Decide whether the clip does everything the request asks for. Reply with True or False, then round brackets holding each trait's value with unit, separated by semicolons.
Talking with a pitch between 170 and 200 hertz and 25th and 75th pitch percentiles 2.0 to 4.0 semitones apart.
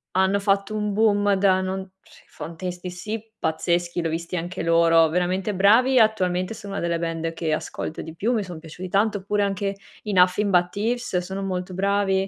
True (190 Hz; 2.6 semitones)